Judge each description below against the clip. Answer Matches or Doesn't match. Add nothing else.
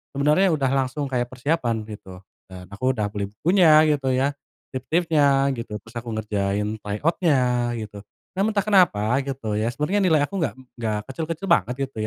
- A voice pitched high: Doesn't match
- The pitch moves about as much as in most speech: Doesn't match